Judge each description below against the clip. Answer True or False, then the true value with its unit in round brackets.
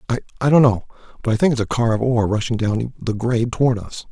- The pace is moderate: False (250 wpm)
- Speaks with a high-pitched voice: False (115 Hz)